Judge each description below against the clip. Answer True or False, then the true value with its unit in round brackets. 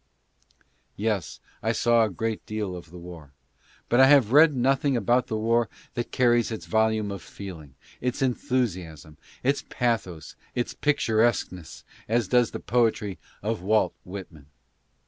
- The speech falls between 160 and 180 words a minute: False (145 wpm)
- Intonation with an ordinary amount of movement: True (4.6 semitones)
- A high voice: False (110 Hz)